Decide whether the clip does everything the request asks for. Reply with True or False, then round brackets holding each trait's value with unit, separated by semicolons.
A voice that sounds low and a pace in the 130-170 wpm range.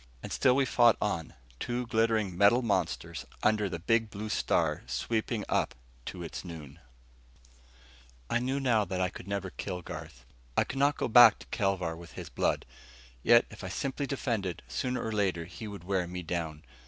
False (100 Hz; 180 wpm)